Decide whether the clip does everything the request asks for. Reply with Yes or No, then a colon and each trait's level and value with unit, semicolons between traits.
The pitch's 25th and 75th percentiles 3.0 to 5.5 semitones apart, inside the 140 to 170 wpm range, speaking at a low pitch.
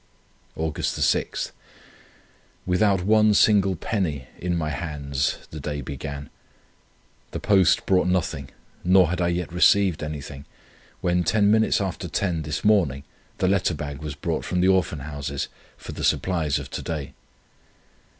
Yes: average, 4.5 semitones; average, 145 wpm; very low, 85 Hz